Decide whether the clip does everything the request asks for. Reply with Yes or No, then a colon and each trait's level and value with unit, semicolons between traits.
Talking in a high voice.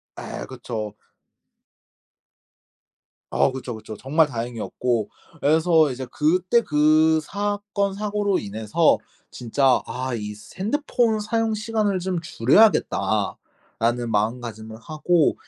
No: medium, 150 Hz